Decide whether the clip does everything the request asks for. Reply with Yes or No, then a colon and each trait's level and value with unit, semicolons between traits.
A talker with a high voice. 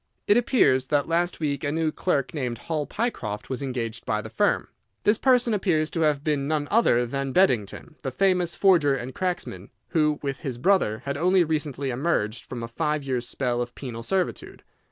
No: medium, 145 Hz